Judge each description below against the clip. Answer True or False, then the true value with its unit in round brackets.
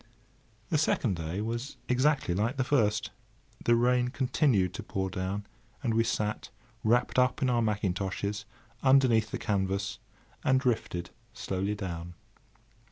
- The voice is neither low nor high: False (110 Hz)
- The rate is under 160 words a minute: True (135 wpm)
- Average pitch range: True (4.5 semitones)